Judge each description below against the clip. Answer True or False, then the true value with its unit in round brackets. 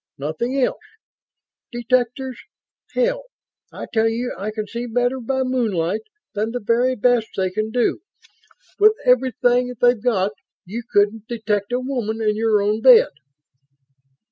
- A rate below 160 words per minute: True (140 wpm)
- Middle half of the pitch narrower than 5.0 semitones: True (2.7 semitones)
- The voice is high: True (235 Hz)